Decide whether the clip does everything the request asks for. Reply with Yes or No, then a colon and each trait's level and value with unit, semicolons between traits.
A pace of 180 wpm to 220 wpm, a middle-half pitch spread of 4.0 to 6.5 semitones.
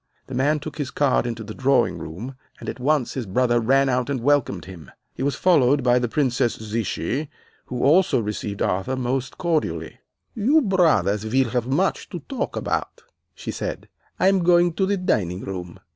Yes: average, 185 wpm; average, 5.2 semitones